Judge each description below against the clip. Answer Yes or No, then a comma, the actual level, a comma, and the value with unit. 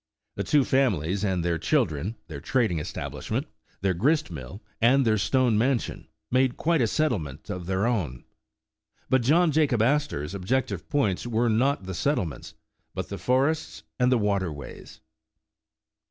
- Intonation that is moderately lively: No, wide, 6.5 semitones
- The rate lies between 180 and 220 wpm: No, average, 155 wpm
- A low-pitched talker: Yes, low, 115 Hz